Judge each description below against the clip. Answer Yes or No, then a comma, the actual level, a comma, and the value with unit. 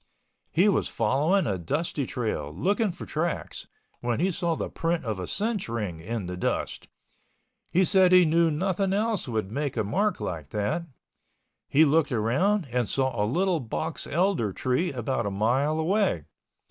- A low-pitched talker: No, medium, 150 Hz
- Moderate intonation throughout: No, wide, 8.4 semitones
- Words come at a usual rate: Yes, average, 170 wpm